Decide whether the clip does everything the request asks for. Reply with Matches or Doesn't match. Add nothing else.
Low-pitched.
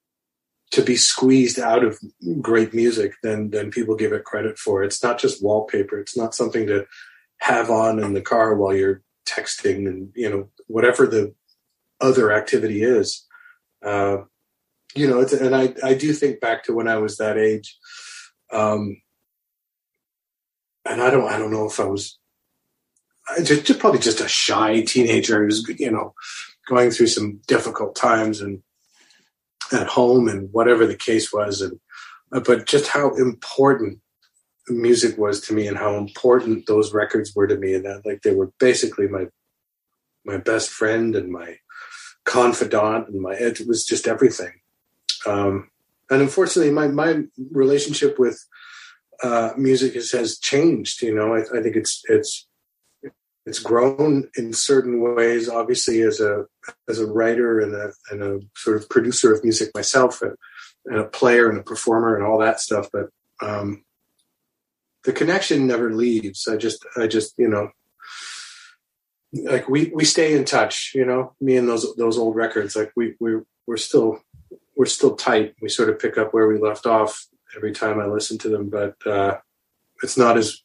Matches